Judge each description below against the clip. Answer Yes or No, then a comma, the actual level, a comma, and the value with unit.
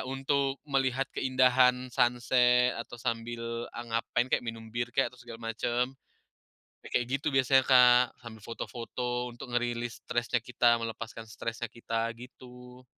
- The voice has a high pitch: No, low, 120 Hz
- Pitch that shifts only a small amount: Yes, narrow, 1.5 semitones